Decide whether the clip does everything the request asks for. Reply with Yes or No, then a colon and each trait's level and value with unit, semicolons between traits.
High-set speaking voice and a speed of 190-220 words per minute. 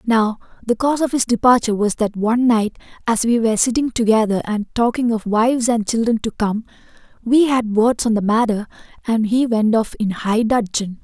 Yes: high, 225 Hz; average, 195 wpm